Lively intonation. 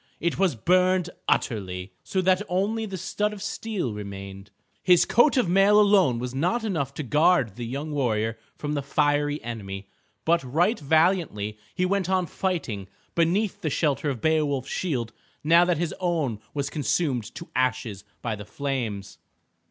Yes: wide, 7.6 semitones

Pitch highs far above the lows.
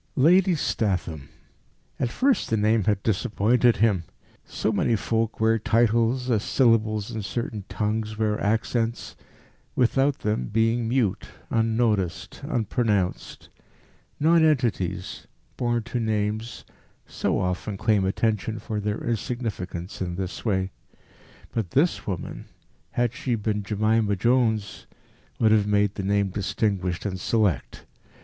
No: average, 2.7 semitones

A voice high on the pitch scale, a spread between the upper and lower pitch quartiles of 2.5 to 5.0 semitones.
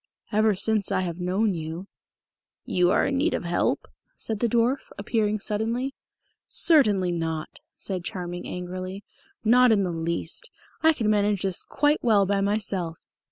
Yes: high, 200 Hz; average, 3.8 semitones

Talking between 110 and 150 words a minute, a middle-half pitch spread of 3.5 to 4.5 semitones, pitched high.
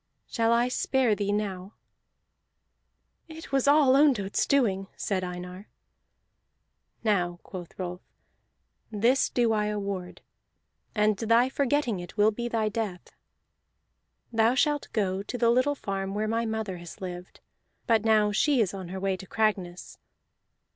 Yes: average, 140 wpm; average, 3.8 semitones; high, 215 Hz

